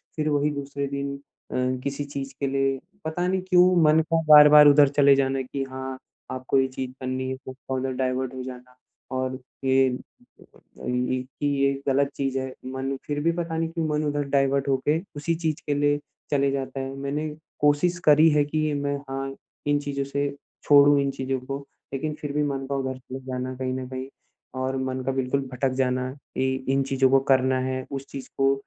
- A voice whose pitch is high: No, low, 135 Hz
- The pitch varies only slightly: Yes, narrow, 1.8 semitones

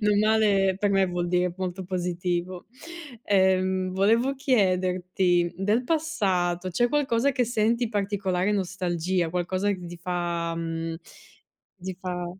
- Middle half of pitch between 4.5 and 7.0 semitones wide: No, average, 2.7 semitones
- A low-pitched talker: No, medium, 185 Hz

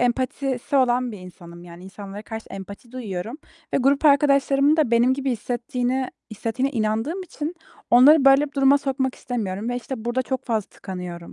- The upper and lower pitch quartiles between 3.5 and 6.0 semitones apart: Yes, average, 4.1 semitones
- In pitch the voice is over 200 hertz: Yes, high, 245 Hz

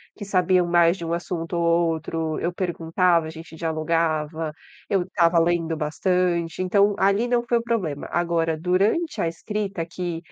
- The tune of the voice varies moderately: No, narrow, 2.1 semitones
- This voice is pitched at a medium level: Yes, medium, 170 Hz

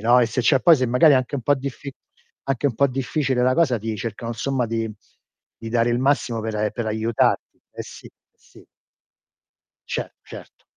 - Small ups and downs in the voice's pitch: No, average, 3.0 semitones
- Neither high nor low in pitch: No, low, 125 Hz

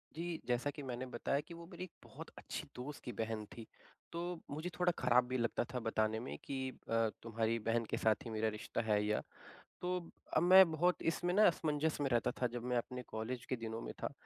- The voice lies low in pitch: Yes, low, 125 Hz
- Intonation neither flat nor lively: No, wide, 6.0 semitones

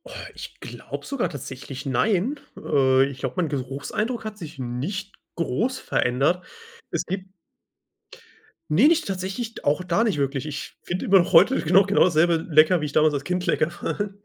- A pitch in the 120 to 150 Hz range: No, medium, 170 Hz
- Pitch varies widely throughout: Yes, wide, 6.0 semitones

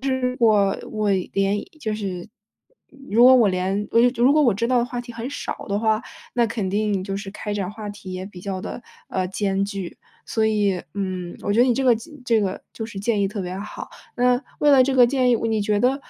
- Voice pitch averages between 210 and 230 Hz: Yes, high, 215 Hz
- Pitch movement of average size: Yes, average, 3.5 semitones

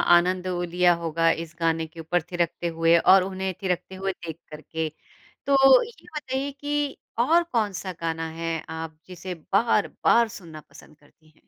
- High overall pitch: No, medium, 180 Hz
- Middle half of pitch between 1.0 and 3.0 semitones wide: No, average, 4.5 semitones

